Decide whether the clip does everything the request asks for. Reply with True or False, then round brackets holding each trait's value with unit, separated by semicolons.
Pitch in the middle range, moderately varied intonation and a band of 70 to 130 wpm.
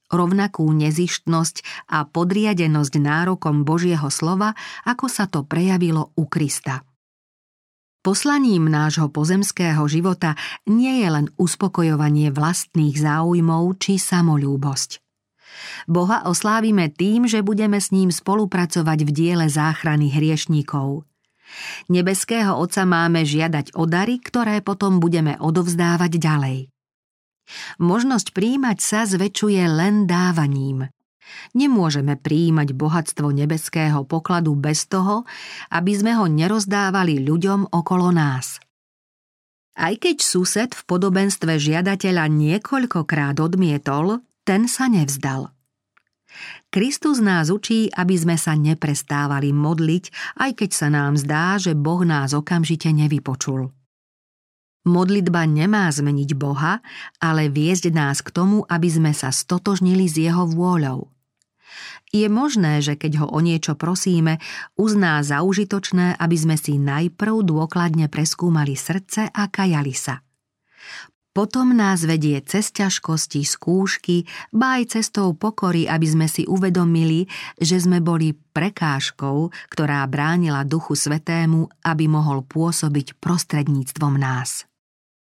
True (165 Hz; 4.1 semitones; 115 wpm)